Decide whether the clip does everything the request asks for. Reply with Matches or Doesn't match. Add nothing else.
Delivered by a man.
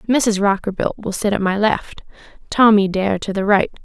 Doesn't match